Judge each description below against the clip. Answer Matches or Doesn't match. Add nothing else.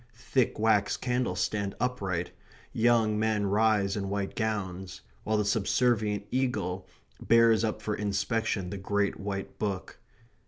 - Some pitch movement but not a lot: Doesn't match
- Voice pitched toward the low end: Matches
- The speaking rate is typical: Doesn't match